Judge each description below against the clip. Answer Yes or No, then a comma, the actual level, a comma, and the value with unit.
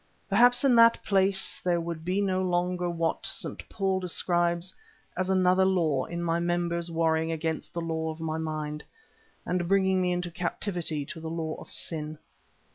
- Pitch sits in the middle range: Yes, medium, 175 Hz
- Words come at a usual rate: Yes, average, 170 wpm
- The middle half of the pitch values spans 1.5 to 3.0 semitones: Yes, narrow, 2.4 semitones